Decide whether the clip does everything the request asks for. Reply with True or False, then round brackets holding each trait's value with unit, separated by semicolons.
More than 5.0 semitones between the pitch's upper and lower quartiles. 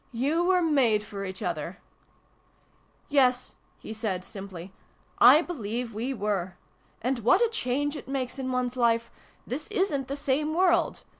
True (5.5 semitones)